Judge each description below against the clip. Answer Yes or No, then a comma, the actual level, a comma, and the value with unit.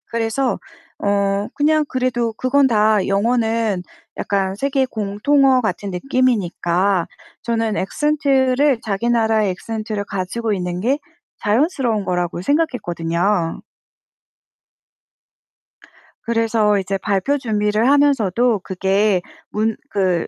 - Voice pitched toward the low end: No, high, 220 Hz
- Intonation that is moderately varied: Yes, average, 4.4 semitones